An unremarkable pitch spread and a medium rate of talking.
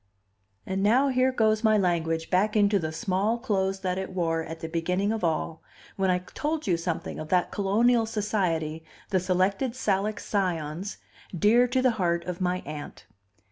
Yes: average, 4.0 semitones; average, 175 wpm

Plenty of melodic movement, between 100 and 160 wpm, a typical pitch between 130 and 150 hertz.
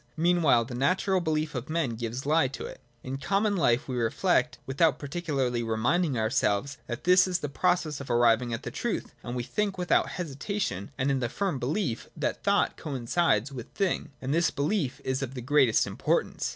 No: wide, 5.8 semitones; average, 195 wpm; medium, 140 Hz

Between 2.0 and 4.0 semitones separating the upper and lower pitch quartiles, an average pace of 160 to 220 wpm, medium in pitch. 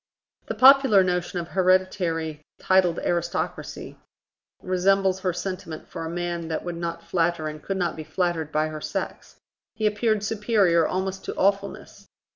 No: narrow, 2.6 semitones; average, 150 wpm; medium, 180 Hz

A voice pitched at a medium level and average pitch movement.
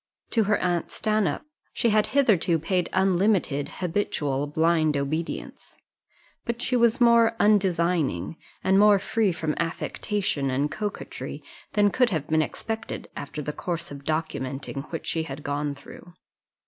No: medium, 170 Hz; wide, 5.9 semitones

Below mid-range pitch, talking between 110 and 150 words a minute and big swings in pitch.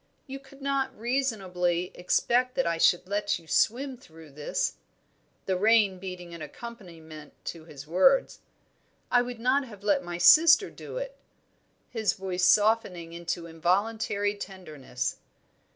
No: high, 195 Hz; slow, 135 wpm; wide, 6.0 semitones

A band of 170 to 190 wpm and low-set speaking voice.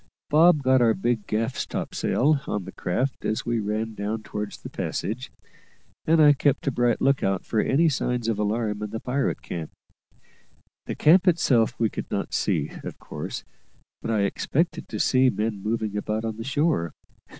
Yes: average, 180 wpm; low, 115 Hz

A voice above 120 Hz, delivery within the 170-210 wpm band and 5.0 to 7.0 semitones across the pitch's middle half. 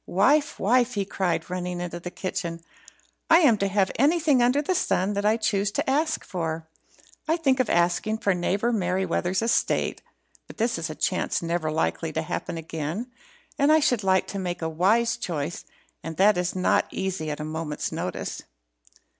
Yes: high, 190 Hz; average, 180 wpm; average, 5.3 semitones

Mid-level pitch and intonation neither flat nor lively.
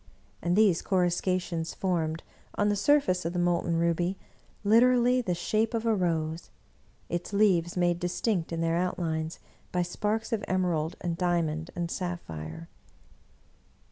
Yes: medium, 175 Hz; average, 3.1 semitones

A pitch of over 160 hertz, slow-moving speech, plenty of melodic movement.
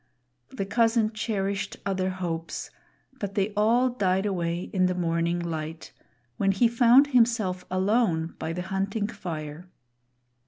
No: high, 190 Hz; slow, 130 wpm; average, 3.8 semitones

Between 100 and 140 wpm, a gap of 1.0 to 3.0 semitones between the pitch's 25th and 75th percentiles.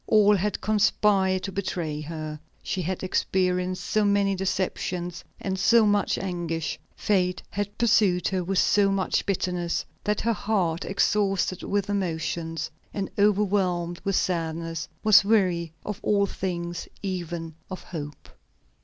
Yes: slow, 135 wpm; average, 2.7 semitones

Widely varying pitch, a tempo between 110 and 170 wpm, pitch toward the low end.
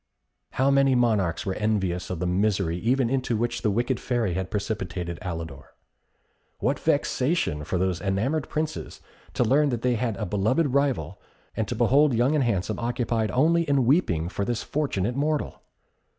Yes: wide, 6.1 semitones; average, 165 wpm; low, 115 Hz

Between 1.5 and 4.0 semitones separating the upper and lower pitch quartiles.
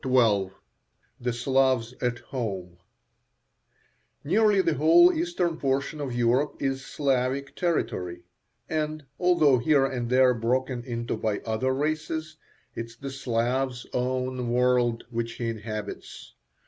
Yes: average, 3.4 semitones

